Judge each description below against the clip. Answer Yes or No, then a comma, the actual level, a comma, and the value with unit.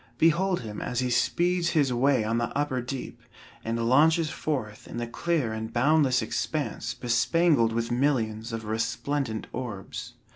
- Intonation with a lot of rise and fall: No, average, 4.3 semitones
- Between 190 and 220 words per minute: No, average, 150 wpm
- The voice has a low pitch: Yes, low, 125 Hz